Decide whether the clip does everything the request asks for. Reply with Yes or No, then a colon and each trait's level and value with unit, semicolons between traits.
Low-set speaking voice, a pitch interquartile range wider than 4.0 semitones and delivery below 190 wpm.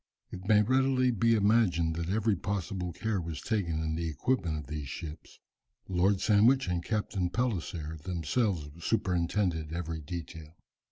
Yes: very low, 90 Hz; average, 4.6 semitones; average, 145 wpm